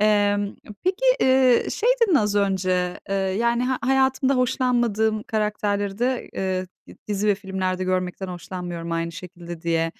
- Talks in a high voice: Yes, high, 205 Hz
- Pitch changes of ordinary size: Yes, average, 4.6 semitones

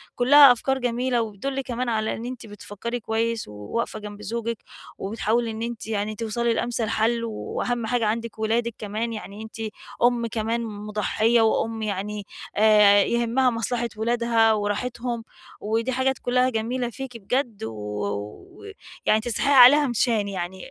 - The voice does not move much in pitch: Yes, narrow, 2.3 semitones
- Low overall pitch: No, high, 230 Hz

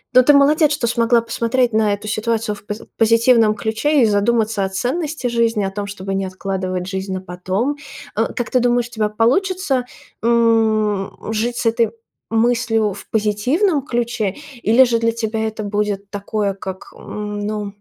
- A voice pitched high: Yes, high, 225 Hz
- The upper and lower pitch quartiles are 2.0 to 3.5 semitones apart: Yes, average, 2.7 semitones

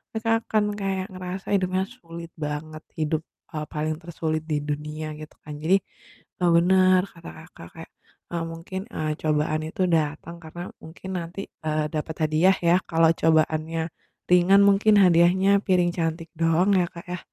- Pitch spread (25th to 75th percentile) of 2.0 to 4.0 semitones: Yes, average, 3.0 semitones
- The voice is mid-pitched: Yes, medium, 170 Hz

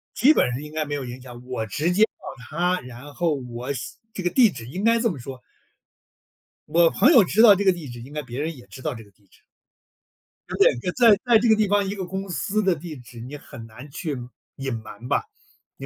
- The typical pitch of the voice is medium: Yes, medium, 150 Hz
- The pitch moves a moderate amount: No, wide, 7.6 semitones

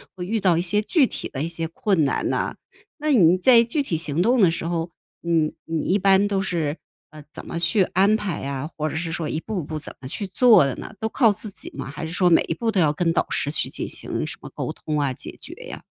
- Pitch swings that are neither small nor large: Yes, average, 4.7 semitones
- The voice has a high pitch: No, medium, 175 Hz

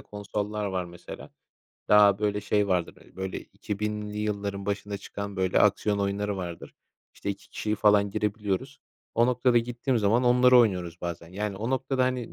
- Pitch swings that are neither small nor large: No, narrow, 1.6 semitones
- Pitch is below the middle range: Yes, low, 105 Hz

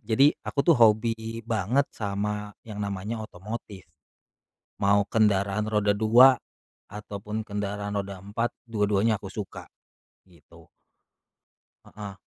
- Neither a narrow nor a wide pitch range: No, narrow, 1.6 semitones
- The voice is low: Yes, low, 105 Hz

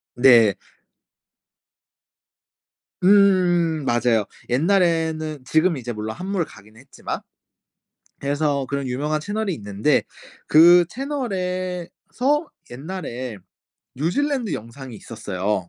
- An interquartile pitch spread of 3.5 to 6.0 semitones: No, wide, 7.1 semitones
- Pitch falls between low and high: Yes, medium, 155 Hz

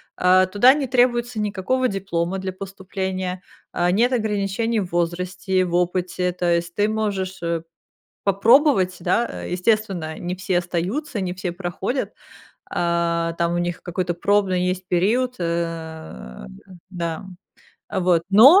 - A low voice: No, medium, 185 Hz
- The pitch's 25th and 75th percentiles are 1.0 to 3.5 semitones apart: Yes, average, 3.0 semitones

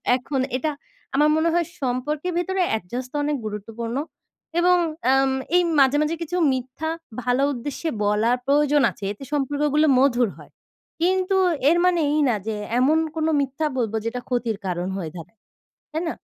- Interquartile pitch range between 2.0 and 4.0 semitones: No, average, 4.6 semitones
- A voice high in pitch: Yes, very high, 270 Hz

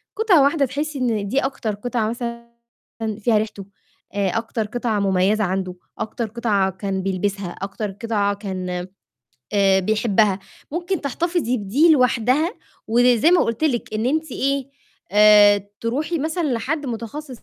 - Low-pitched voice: No, high, 230 Hz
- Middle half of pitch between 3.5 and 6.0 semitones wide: Yes, average, 5.2 semitones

